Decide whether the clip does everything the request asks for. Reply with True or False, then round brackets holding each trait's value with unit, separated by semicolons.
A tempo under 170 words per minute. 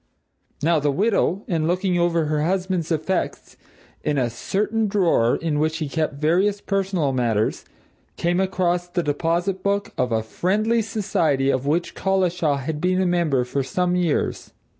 True (160 wpm)